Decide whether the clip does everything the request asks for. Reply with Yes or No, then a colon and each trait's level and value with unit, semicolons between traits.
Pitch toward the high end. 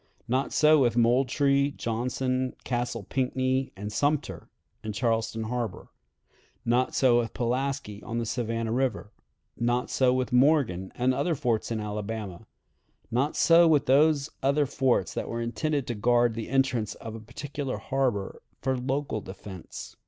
No: low, 125 Hz